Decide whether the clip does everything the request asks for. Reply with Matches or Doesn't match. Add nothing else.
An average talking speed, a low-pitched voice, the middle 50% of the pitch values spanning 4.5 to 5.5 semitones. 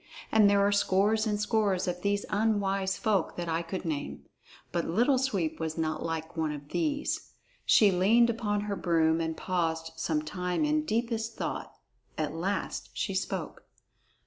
Doesn't match